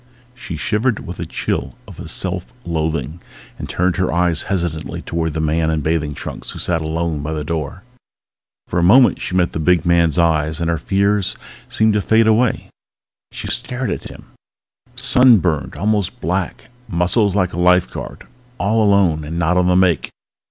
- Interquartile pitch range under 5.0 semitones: Yes, average, 3.6 semitones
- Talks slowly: No, average, 175 wpm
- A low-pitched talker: Yes, very low, 85 Hz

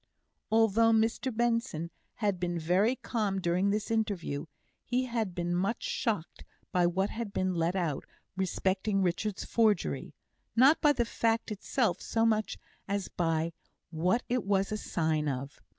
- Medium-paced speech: Yes, average, 150 wpm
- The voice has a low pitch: No, high, 200 Hz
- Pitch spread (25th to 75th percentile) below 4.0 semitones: No, average, 4.5 semitones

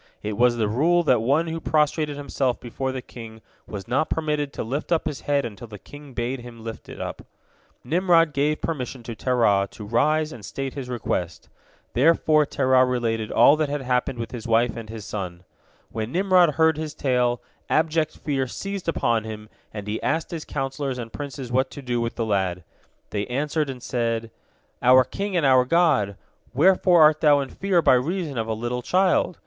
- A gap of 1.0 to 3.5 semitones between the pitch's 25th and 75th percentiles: No, average, 4.8 semitones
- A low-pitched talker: Yes, low, 130 Hz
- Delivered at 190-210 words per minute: Yes, average, 195 wpm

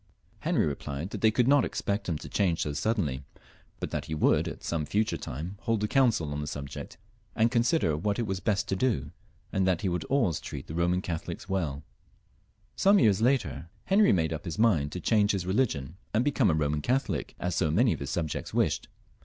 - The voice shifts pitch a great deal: Yes, wide, 6.3 semitones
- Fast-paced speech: Yes, fast, 215 wpm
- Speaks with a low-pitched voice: Yes, very low, 95 Hz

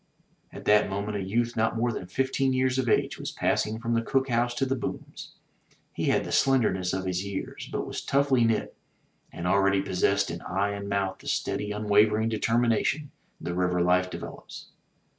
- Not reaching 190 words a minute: No, average, 195 wpm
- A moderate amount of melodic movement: Yes, average, 3.8 semitones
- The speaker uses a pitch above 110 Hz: No, low, 105 Hz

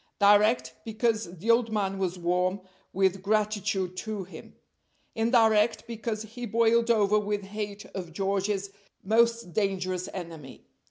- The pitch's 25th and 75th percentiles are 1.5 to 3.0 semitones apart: Yes, narrow, 2.6 semitones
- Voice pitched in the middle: No, high, 205 Hz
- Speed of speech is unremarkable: No, slow, 125 wpm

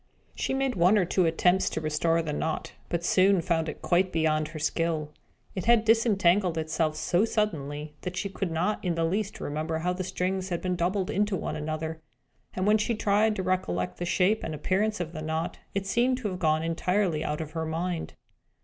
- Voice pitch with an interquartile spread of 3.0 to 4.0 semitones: Yes, average, 3.5 semitones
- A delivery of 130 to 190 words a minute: No, fast, 205 wpm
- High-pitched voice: No, medium, 175 Hz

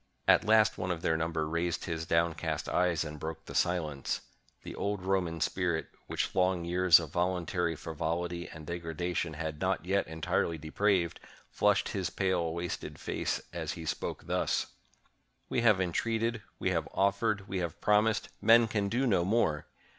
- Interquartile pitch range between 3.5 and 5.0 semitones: No, average, 3.1 semitones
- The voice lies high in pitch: No, very low, 90 Hz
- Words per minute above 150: Yes, average, 175 wpm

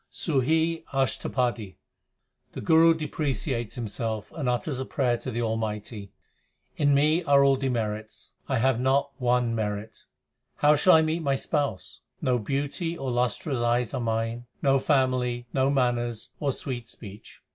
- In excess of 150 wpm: No, average, 145 wpm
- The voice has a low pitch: Yes, low, 125 Hz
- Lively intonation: No, average, 3.3 semitones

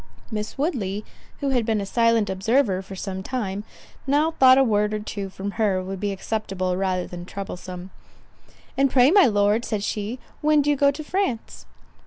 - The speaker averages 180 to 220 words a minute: Yes, average, 185 wpm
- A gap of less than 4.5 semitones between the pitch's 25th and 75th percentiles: No, average, 5.2 semitones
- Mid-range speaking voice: No, high, 210 Hz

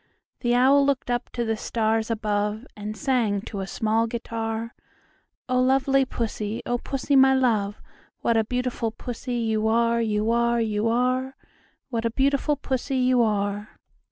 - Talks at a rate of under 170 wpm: Yes, average, 155 wpm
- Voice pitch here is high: Yes, high, 235 Hz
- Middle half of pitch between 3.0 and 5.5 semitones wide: No, narrow, 2.6 semitones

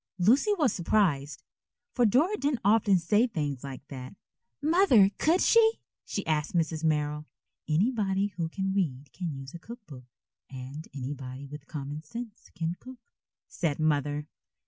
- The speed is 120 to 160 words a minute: Yes, average, 145 wpm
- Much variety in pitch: Yes, wide, 7.1 semitones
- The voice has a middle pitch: Yes, medium, 165 Hz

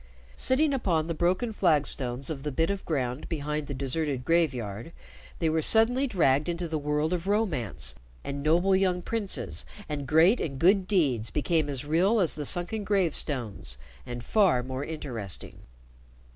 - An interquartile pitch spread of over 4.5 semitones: Yes, average, 5.2 semitones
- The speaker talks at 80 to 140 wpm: No, average, 160 wpm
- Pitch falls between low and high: Yes, medium, 160 Hz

